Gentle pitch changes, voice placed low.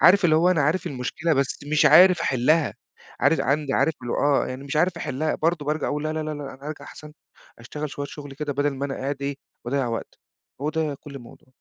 No: narrow, 2.3 semitones; medium, 145 Hz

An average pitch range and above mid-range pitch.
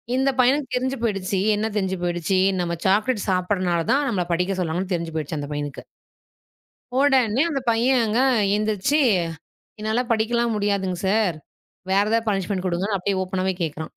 Yes: average, 4.2 semitones; high, 200 Hz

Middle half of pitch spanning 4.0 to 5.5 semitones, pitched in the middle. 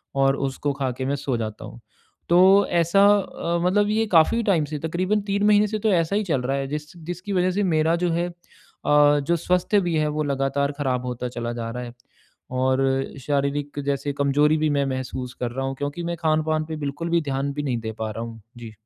Yes: average, 4.4 semitones; medium, 145 Hz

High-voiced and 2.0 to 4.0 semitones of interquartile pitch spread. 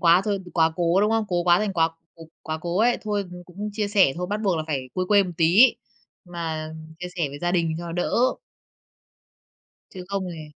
No: medium, 175 Hz; average, 3.5 semitones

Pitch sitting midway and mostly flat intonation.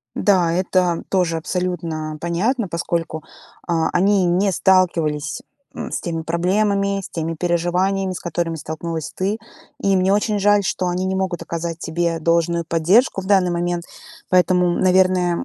Yes: medium, 175 Hz; narrow, 2.2 semitones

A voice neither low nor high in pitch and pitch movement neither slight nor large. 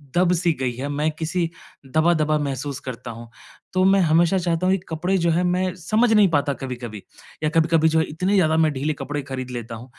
Yes: medium, 160 Hz; average, 4.4 semitones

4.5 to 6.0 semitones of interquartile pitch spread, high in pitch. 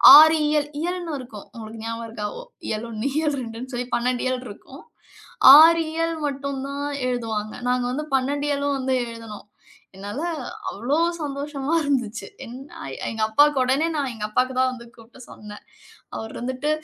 No: average, 4.0 semitones; very high, 255 Hz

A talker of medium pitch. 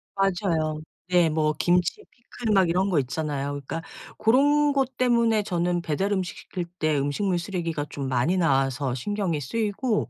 Yes: medium, 175 Hz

